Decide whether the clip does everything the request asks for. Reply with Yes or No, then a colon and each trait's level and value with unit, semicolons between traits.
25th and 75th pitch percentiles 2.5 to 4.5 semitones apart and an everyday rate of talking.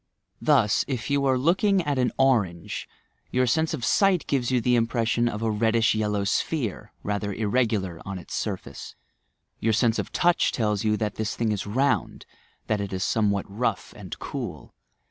Yes: average, 3.8 semitones; average, 180 wpm